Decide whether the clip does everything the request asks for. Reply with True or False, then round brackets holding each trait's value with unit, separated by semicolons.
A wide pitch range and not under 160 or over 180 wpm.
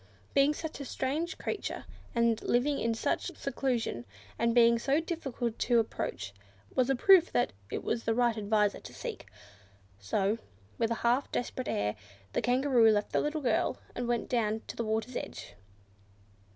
False (3.3 semitones; 165 wpm)